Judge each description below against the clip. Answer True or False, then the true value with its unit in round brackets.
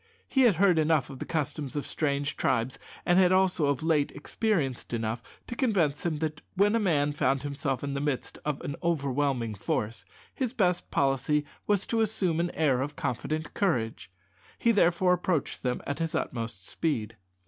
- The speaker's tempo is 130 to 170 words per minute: False (180 wpm)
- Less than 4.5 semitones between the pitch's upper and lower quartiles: False (4.8 semitones)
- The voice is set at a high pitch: False (150 Hz)